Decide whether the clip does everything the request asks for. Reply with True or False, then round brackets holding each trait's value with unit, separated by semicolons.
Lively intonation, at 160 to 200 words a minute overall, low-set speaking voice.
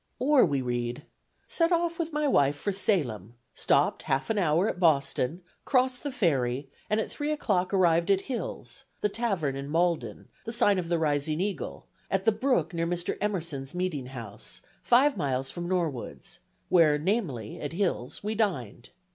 False (7.2 semitones; 170 wpm; 175 Hz)